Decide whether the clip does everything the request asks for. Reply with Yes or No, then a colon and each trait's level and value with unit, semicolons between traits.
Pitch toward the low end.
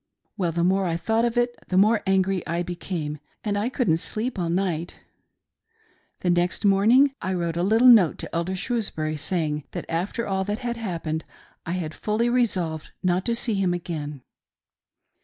No: medium, 185 Hz